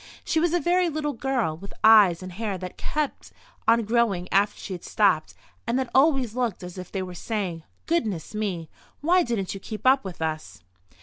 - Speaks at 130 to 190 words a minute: No, average, 200 wpm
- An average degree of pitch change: No, wide, 6.3 semitones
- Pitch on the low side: No, high, 215 Hz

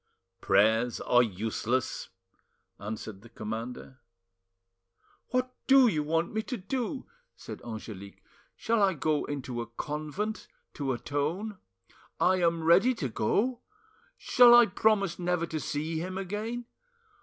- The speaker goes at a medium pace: No, slow, 125 wpm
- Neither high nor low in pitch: Yes, medium, 165 Hz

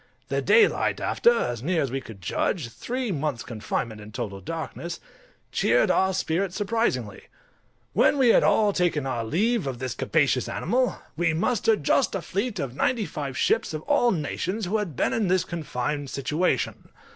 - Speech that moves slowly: No, average, 170 wpm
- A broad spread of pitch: Yes, wide, 7.7 semitones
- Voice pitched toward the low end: No, medium, 165 Hz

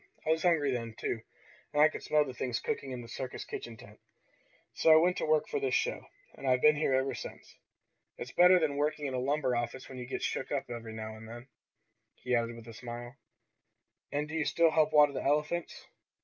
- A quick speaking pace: Yes, fast, 225 wpm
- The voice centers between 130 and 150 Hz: Yes, low, 135 Hz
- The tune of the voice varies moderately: Yes, average, 4.1 semitones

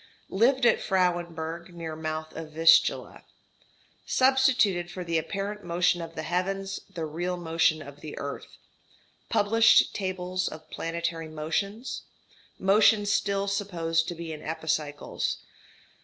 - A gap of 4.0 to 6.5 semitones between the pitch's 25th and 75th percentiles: No, average, 3.4 semitones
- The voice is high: No, medium, 175 Hz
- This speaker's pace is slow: Yes, slow, 125 wpm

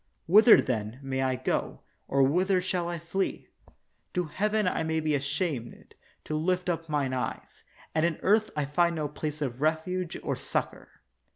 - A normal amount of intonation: Yes, average, 4.3 semitones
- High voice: No, medium, 160 Hz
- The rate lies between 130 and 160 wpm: No, average, 170 wpm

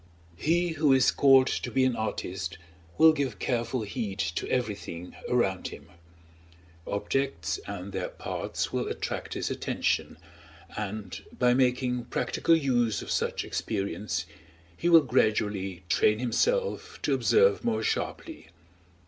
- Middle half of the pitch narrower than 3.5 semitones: No, average, 5.0 semitones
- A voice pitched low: Yes, low, 120 Hz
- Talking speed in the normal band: No, slow, 130 wpm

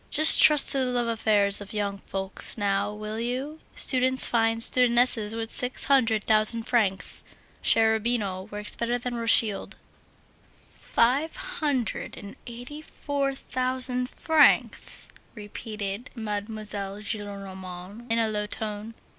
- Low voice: No, high, 225 Hz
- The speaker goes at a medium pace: No, slow, 120 wpm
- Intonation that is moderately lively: Yes, average, 3.3 semitones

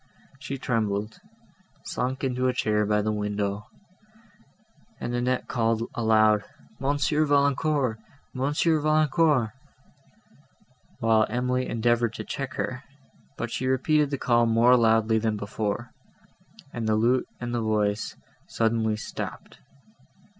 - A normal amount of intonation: Yes, average, 3.2 semitones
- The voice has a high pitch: No, low, 120 Hz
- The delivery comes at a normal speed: No, slow, 120 wpm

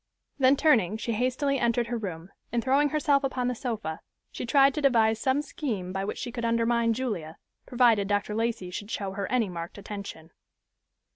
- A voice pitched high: Yes, high, 230 Hz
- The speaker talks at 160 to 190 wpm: Yes, average, 185 wpm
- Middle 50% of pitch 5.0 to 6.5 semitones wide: No, average, 4.2 semitones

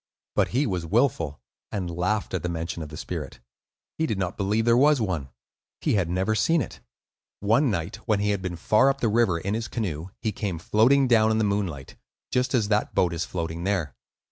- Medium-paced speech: No, fast, 215 wpm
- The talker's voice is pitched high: No, low, 100 Hz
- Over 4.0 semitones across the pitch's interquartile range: Yes, average, 4.6 semitones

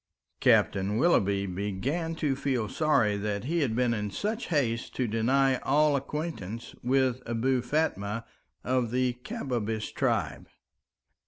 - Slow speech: Yes, slow, 130 wpm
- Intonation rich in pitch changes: No, average, 4.8 semitones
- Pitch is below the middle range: Yes, low, 125 Hz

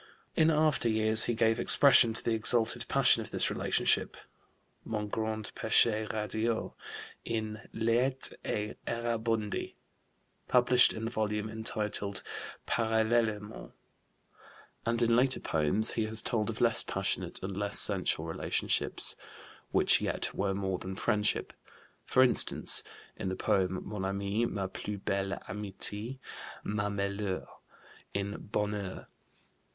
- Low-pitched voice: Yes, low, 110 Hz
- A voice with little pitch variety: Yes, narrow, 2.2 semitones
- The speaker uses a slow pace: Yes, slow, 125 wpm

